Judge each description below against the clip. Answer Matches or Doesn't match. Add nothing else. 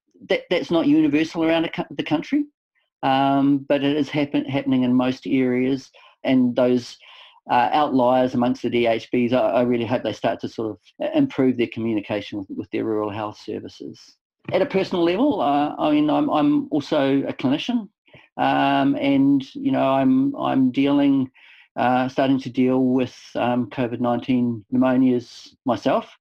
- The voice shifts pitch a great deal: Matches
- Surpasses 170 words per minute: Doesn't match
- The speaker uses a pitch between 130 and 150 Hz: Matches